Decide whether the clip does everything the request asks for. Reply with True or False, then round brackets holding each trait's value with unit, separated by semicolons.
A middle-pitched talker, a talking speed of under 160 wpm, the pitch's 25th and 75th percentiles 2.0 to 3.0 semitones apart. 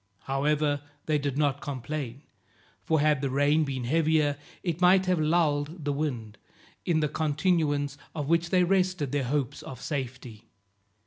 True (145 Hz; 150 wpm; 2.4 semitones)